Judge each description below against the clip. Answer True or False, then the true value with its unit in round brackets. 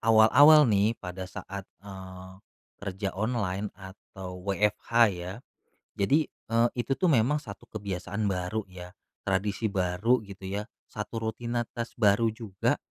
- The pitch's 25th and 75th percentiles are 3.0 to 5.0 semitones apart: True (3.3 semitones)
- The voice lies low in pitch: True (100 Hz)